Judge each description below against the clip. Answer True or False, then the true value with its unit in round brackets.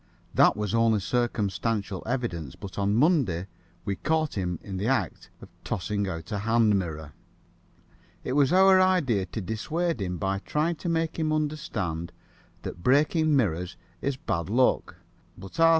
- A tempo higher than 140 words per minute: True (155 wpm)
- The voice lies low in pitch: True (110 Hz)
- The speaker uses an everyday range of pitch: False (8.0 semitones)